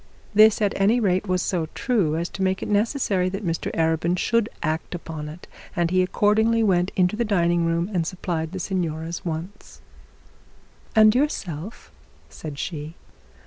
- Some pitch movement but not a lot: Yes, average, 3.9 semitones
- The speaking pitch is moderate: Yes, medium, 180 Hz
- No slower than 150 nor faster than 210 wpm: Yes, average, 165 wpm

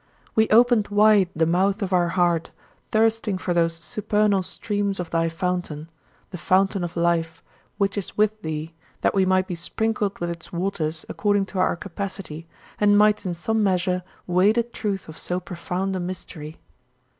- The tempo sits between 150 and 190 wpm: Yes, average, 170 wpm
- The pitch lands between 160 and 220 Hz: Yes, medium, 185 Hz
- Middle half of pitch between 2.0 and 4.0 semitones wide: Yes, average, 3.1 semitones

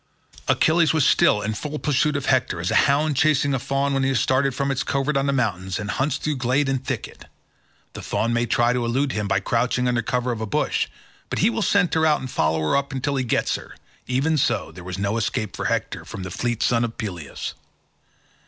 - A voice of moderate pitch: No, low, 130 Hz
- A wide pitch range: No, average, 3.9 semitones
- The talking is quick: Yes, fast, 230 wpm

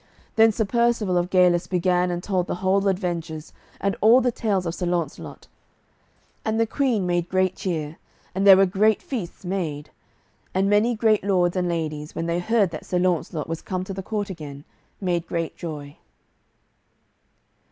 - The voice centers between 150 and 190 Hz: Yes, medium, 185 Hz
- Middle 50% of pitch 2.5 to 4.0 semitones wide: Yes, average, 3.0 semitones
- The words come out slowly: No, average, 175 wpm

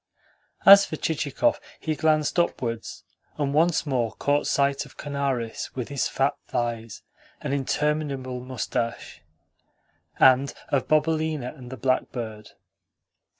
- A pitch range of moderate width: Yes, average, 3.4 semitones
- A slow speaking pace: Yes, slow, 115 wpm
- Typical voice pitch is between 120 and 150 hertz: Yes, medium, 140 Hz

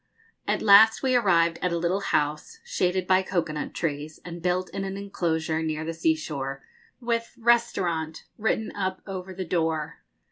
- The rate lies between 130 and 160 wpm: No, average, 170 wpm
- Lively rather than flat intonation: No, average, 3.7 semitones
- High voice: No, medium, 180 Hz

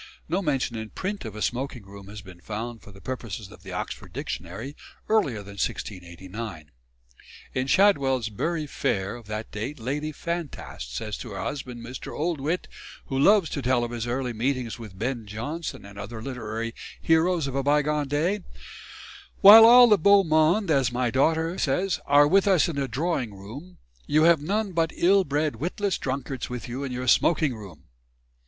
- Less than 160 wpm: No, average, 180 wpm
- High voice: No, low, 135 Hz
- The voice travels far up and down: Yes, wide, 6.4 semitones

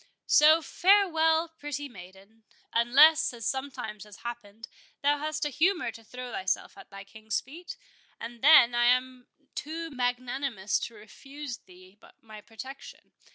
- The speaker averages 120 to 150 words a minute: Yes, average, 140 wpm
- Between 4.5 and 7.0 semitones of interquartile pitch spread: Yes, average, 5.3 semitones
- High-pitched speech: Yes, very high, 250 Hz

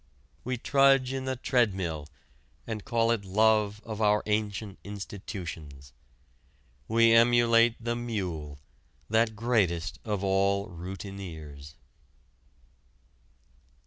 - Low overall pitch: Yes, low, 105 Hz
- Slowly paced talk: Yes, slow, 95 wpm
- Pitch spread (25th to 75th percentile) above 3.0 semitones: Yes, average, 3.7 semitones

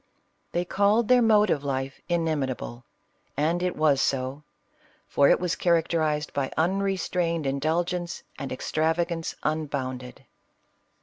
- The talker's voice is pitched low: No, medium, 160 Hz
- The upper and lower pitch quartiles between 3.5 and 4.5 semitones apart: Yes, average, 4.0 semitones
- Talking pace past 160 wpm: No, slow, 135 wpm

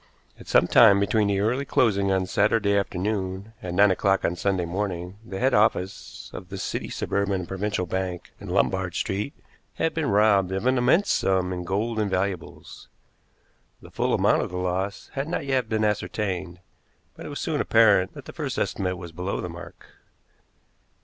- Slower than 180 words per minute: No, average, 185 wpm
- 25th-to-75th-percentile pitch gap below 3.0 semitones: Yes, narrow, 2.6 semitones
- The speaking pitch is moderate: No, low, 100 Hz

